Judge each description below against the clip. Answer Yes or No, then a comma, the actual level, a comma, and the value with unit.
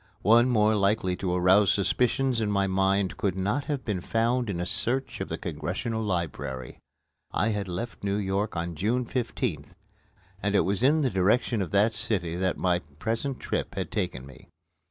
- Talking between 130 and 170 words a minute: No, average, 180 wpm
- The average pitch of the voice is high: No, low, 100 Hz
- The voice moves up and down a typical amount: Yes, average, 4.1 semitones